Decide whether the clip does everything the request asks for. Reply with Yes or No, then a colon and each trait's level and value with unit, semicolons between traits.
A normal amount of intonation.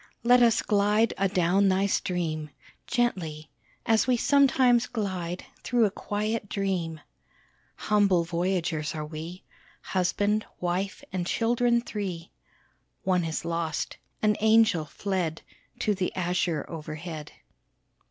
Yes: average, 4.2 semitones